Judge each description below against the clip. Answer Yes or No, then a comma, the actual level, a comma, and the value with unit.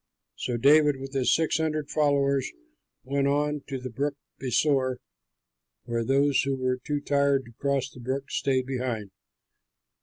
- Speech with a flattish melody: Yes, narrow, 2.0 semitones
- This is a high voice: No, low, 135 Hz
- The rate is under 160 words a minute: Yes, average, 150 wpm